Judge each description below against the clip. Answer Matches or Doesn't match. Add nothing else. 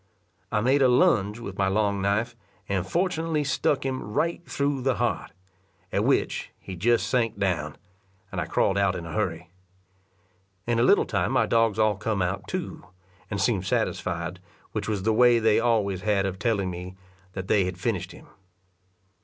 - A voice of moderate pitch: Doesn't match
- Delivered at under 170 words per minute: Doesn't match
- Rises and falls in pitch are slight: Doesn't match